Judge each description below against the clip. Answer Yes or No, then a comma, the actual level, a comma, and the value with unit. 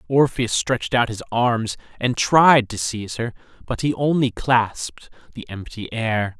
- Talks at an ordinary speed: Yes, average, 160 wpm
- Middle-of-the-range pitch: No, low, 115 Hz